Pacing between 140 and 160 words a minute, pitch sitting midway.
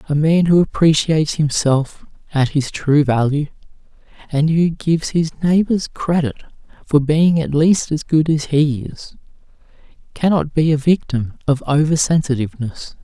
Yes: average, 145 wpm; medium, 150 Hz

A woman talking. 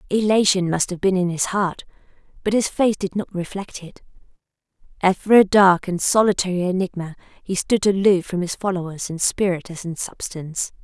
Yes: female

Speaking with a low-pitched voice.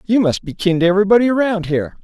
No: high, 195 Hz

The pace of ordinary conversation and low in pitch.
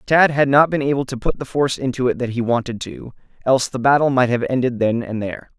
No: fast, 260 wpm; low, 125 Hz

